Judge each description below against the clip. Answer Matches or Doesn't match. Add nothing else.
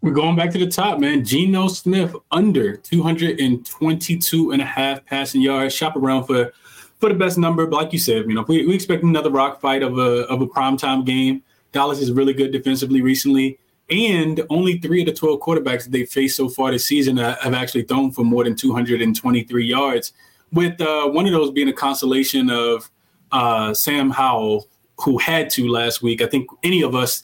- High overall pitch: Doesn't match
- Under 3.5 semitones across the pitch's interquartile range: Doesn't match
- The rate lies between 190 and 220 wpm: Matches